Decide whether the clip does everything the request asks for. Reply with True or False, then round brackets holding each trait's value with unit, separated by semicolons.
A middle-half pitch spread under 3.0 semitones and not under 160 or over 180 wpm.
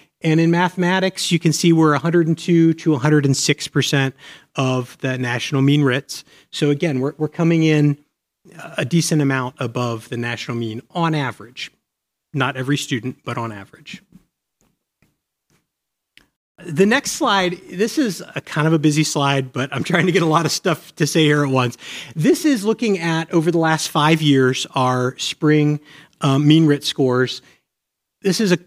False (3.9 semitones; 165 wpm)